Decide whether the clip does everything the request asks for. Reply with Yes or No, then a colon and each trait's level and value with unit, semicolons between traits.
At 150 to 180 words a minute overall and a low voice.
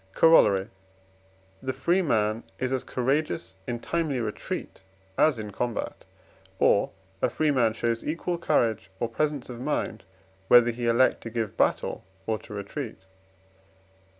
No: average, 140 wpm; low, 120 Hz